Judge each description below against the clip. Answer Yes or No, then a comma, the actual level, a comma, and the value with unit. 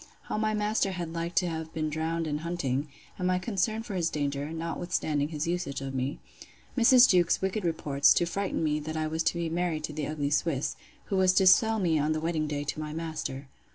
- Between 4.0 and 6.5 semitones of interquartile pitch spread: No, average, 3.1 semitones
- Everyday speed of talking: No, fast, 225 wpm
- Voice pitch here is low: No, medium, 165 Hz